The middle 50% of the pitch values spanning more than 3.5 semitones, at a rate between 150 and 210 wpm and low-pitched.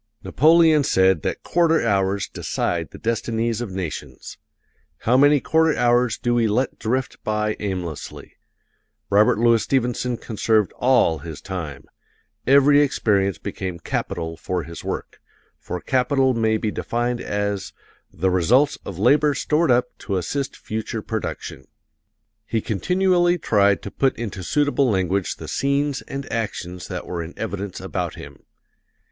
No: wide, 5.6 semitones; average, 140 wpm; low, 115 Hz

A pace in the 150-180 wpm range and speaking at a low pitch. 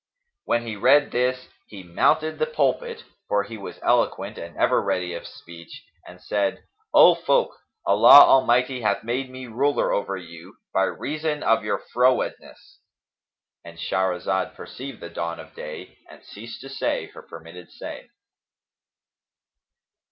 No: average, 140 wpm; low, 115 Hz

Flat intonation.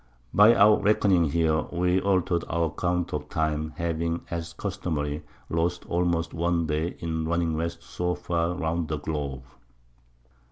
Yes: narrow, 1.7 semitones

